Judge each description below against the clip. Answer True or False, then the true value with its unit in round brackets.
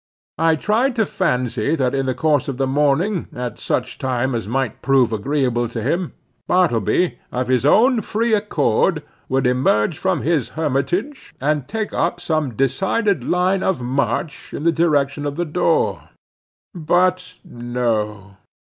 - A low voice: False (145 Hz)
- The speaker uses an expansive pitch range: True (6.0 semitones)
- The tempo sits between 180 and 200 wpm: False (150 wpm)